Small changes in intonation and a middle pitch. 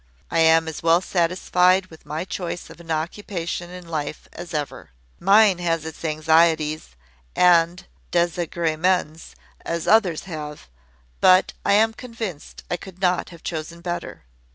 Yes: narrow, 2.2 semitones; medium, 170 Hz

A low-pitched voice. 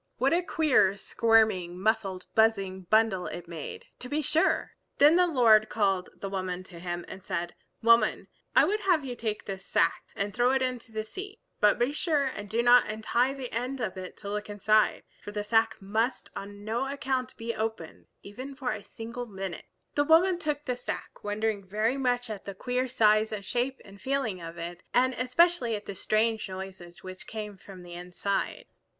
No: high, 220 Hz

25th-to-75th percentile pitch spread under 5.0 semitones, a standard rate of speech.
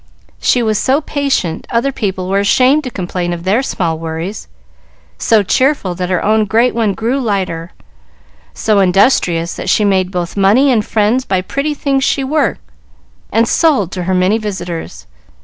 No: wide, 5.5 semitones; average, 165 wpm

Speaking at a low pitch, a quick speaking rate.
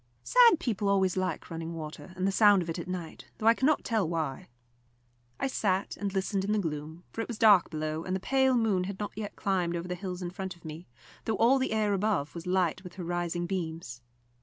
No: medium, 185 Hz; fast, 235 wpm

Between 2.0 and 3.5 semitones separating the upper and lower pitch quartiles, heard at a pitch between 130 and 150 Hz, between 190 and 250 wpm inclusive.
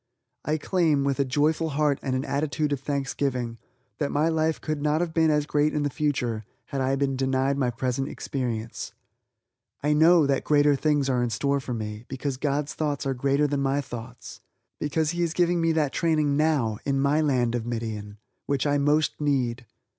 Yes: average, 2.7 semitones; medium, 140 Hz; average, 195 wpm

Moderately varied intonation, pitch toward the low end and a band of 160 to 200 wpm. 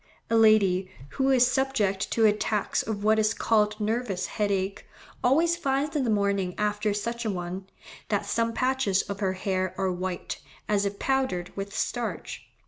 No: average, 3.5 semitones; high, 210 Hz; average, 165 wpm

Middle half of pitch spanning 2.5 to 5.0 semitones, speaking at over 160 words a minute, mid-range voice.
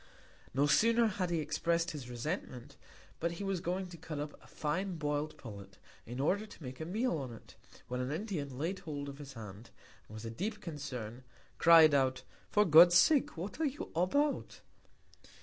No: wide, 5.6 semitones; average, 180 wpm; medium, 155 Hz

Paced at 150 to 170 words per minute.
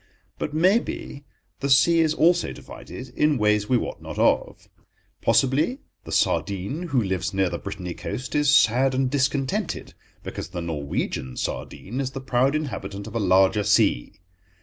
Yes: average, 155 wpm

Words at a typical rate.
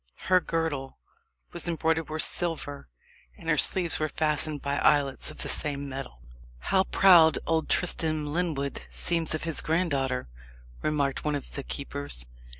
Yes: average, 150 wpm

